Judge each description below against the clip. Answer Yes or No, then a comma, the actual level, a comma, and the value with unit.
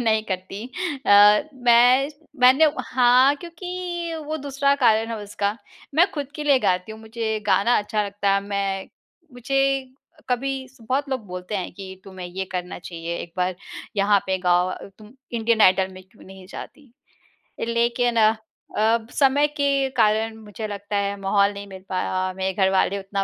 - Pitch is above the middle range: Yes, high, 215 Hz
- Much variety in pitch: No, average, 4.9 semitones